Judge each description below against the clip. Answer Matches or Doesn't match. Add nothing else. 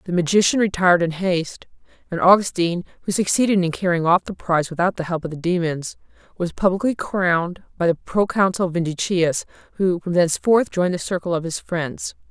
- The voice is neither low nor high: Matches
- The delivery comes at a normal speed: Matches